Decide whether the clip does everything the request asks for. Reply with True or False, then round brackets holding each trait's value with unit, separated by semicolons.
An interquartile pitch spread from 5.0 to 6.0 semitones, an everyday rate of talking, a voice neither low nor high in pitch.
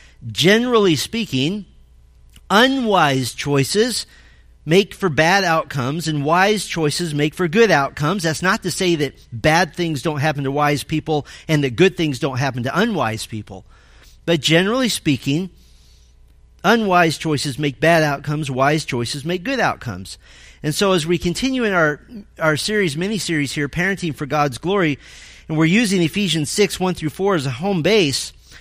True (5.3 semitones; 160 wpm; 155 Hz)